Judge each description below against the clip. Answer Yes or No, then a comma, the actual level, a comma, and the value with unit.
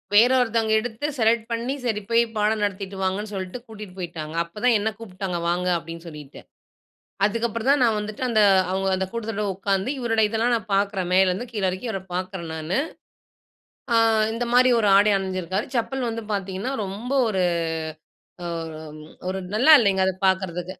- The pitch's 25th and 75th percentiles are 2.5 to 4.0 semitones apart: Yes, average, 3.5 semitones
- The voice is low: No, high, 205 Hz